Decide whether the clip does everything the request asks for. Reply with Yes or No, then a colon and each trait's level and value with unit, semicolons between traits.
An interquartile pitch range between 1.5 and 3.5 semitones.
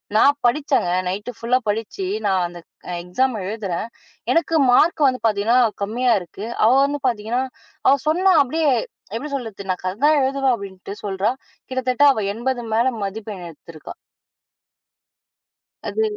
No: average, 4.9 semitones